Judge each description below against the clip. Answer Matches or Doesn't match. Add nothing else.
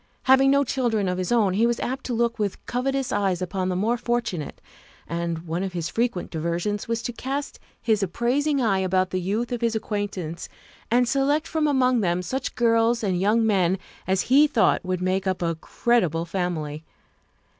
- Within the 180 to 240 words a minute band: Matches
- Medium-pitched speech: Doesn't match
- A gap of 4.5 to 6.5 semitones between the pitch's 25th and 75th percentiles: Matches